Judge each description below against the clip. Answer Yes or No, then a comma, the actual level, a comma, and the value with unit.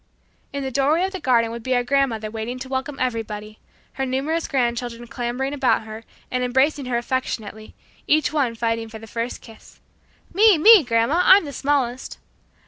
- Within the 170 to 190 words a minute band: Yes, average, 175 wpm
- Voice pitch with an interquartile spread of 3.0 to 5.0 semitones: Yes, average, 3.4 semitones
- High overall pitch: Yes, very high, 255 Hz